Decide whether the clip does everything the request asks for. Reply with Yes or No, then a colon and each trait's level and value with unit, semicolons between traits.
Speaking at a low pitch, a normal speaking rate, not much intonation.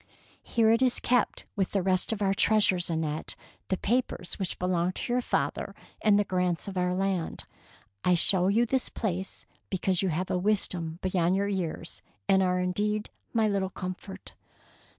No: high, 190 Hz; average, 180 wpm; narrow, 2.3 semitones